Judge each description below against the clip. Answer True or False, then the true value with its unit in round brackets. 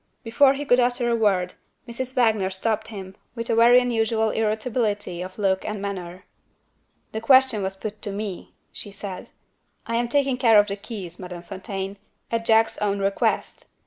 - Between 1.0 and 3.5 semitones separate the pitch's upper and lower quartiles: True (3.1 semitones)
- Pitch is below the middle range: False (215 Hz)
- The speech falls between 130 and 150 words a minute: False (175 wpm)